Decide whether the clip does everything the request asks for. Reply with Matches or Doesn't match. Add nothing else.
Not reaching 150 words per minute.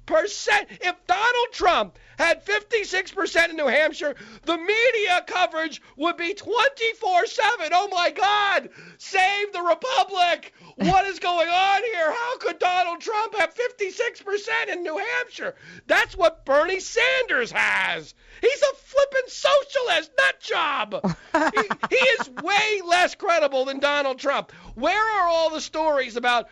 Matches